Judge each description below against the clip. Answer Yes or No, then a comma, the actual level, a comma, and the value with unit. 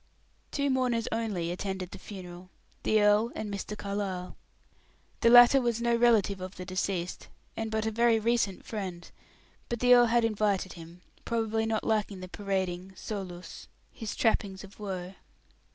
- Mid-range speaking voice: No, high, 205 Hz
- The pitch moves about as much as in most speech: Yes, average, 3.4 semitones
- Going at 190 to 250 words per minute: No, average, 155 wpm